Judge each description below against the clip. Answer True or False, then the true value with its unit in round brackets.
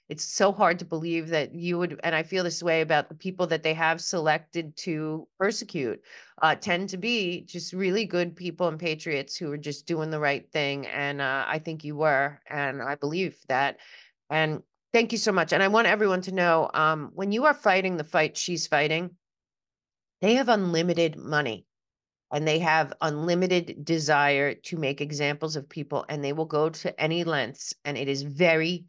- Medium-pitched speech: True (160 Hz)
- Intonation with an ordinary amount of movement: True (3.1 semitones)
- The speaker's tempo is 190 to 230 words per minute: True (195 wpm)